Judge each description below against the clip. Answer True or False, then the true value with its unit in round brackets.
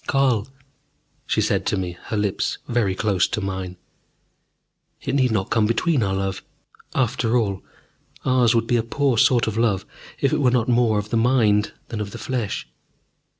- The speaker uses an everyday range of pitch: True (3.3 semitones)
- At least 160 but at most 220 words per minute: True (180 wpm)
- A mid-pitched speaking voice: False (115 Hz)